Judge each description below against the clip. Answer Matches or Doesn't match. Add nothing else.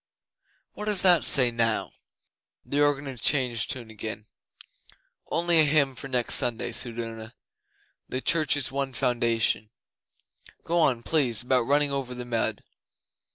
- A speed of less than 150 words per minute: Matches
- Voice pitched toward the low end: Matches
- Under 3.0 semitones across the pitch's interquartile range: Doesn't match